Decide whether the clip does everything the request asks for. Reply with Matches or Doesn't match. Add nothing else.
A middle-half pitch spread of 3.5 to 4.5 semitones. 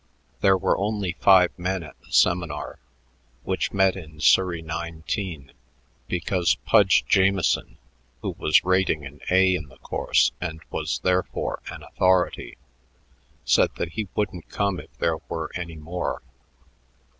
Doesn't match